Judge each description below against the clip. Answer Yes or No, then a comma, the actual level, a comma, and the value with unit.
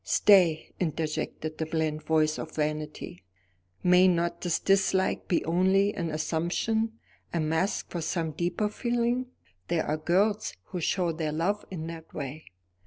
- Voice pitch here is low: No, medium, 170 Hz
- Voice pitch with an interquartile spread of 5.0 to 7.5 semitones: No, average, 3.3 semitones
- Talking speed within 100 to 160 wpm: Yes, average, 145 wpm